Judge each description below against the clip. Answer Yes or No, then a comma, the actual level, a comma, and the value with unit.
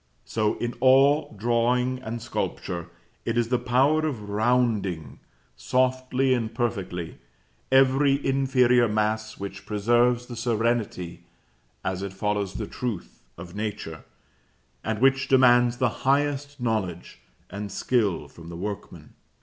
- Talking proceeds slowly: Yes, slow, 125 wpm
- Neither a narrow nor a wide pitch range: Yes, average, 4.0 semitones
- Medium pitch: No, low, 120 Hz